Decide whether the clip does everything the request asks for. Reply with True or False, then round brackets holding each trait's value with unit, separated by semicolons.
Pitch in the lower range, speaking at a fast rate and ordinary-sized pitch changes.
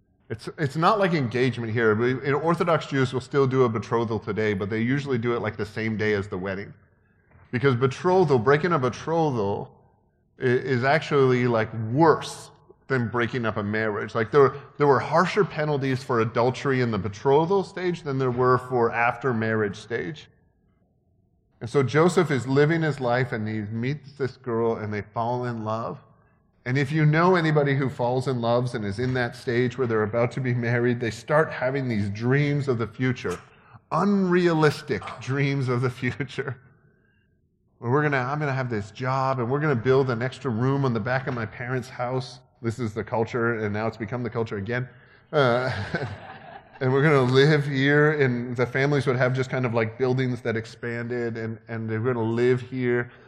False (125 Hz; 190 wpm; 3.3 semitones)